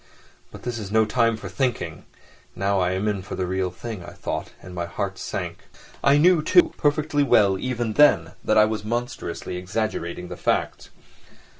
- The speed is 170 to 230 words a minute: Yes, average, 180 wpm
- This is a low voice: Yes, low, 105 Hz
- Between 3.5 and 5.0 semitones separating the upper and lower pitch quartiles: Yes, average, 4.7 semitones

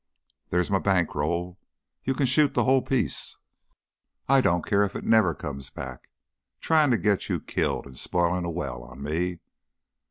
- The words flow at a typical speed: Yes, average, 170 wpm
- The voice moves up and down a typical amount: No, wide, 6.6 semitones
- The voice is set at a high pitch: No, very low, 90 Hz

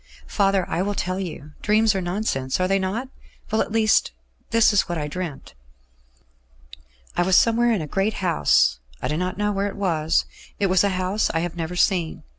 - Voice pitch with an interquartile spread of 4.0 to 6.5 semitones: No, average, 3.0 semitones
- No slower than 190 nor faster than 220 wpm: Yes, average, 200 wpm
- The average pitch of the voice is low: No, high, 190 Hz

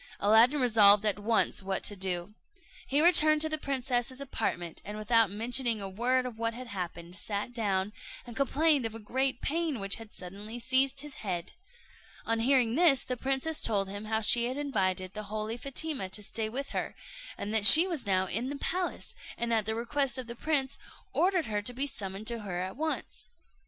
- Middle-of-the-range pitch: No, high, 230 Hz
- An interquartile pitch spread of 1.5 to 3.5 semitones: No, average, 4.7 semitones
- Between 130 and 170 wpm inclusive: No, average, 200 wpm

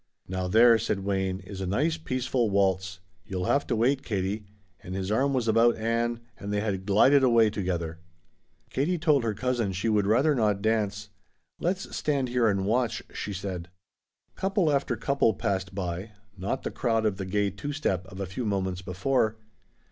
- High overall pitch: No, low, 105 Hz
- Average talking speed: Yes, average, 180 wpm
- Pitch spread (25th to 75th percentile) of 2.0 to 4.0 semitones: No, average, 4.6 semitones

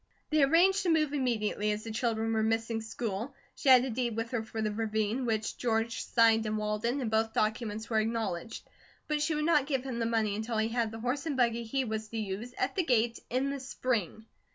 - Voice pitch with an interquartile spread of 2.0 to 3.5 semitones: Yes, average, 2.9 semitones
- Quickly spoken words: Yes, fast, 225 wpm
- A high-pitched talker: Yes, high, 230 Hz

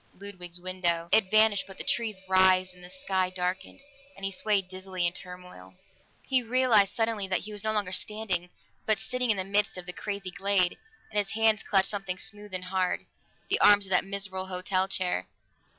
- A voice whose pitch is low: No, high, 190 Hz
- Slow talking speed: No, average, 195 wpm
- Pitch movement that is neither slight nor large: No, narrow, 2.2 semitones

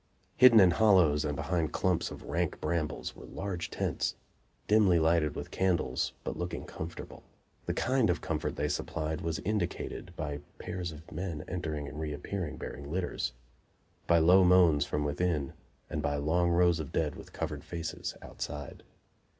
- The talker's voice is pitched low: Yes, very low, 85 Hz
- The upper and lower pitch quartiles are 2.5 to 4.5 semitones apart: Yes, average, 3.1 semitones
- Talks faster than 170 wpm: No, average, 160 wpm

